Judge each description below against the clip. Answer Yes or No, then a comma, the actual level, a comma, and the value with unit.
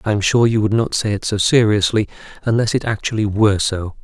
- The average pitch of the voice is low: Yes, low, 105 Hz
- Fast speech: Yes, fast, 225 wpm